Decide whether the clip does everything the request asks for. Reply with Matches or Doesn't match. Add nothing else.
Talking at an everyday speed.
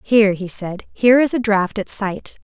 Doesn't match